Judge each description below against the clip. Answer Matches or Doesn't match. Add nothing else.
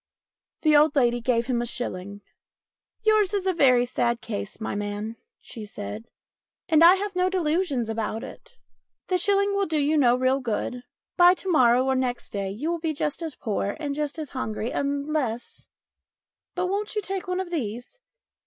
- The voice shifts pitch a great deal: Matches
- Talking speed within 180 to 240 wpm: Matches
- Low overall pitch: Doesn't match